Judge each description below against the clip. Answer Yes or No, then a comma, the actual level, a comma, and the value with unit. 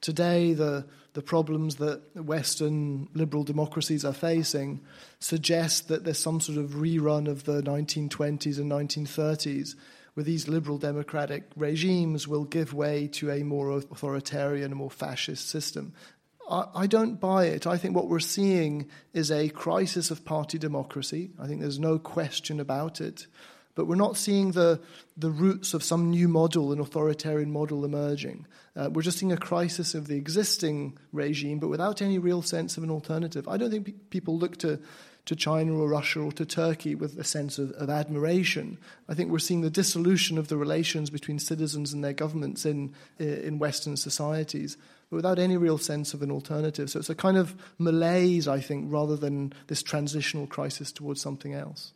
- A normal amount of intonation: No, narrow, 2.2 semitones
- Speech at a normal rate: Yes, average, 180 wpm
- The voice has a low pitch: No, medium, 155 Hz